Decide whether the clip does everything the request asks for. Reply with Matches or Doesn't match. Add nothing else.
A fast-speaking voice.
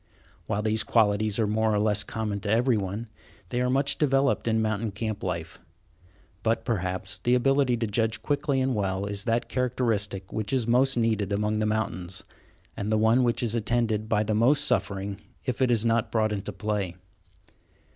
Doesn't match